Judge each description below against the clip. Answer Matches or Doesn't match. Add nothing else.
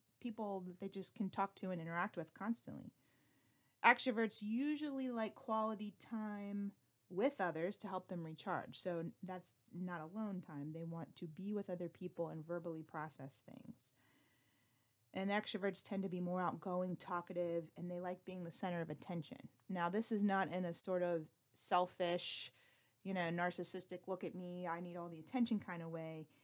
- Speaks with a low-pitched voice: Doesn't match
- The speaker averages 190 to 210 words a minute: Doesn't match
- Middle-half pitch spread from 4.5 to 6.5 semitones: Doesn't match